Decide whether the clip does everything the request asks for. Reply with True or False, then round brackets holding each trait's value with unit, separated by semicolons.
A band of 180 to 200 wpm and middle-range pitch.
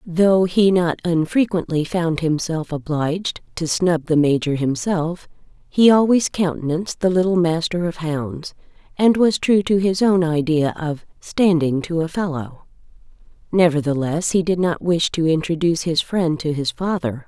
False (155 wpm; 170 Hz)